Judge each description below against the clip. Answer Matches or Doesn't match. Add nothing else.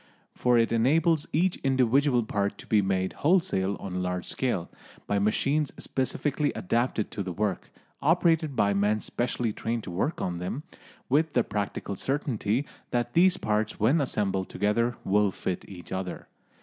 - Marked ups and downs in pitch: Matches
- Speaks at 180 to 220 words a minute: Doesn't match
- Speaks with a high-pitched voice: Doesn't match